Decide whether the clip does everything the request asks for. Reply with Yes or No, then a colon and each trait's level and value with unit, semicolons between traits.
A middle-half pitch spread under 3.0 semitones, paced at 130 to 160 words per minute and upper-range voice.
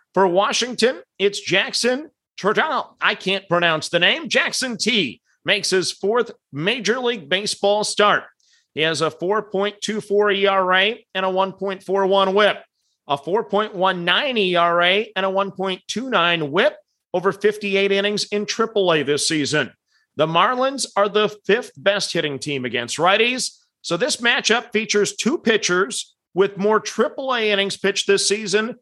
Yes: narrow, 2.5 semitones; slow, 135 wpm; high, 200 Hz